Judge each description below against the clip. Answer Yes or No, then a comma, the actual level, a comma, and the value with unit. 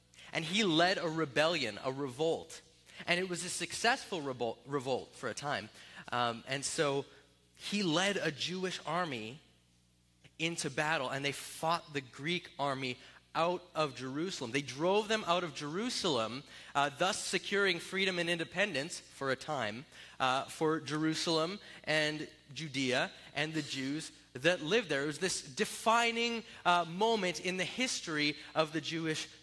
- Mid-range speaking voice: Yes, medium, 155 Hz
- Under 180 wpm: Yes, average, 150 wpm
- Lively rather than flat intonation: No, average, 4.6 semitones